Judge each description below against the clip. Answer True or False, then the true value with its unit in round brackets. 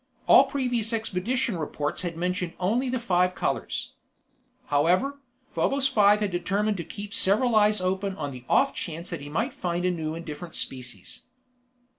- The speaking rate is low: False (165 wpm)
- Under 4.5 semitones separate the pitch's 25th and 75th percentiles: False (4.8 semitones)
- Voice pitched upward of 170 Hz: True (190 Hz)